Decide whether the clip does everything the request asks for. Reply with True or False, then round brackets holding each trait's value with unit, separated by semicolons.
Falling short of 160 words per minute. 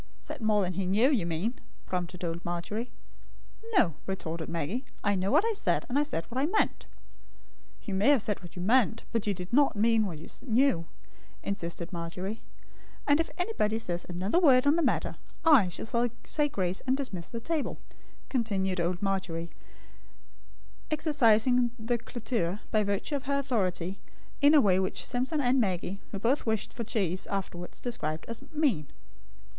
False (170 wpm)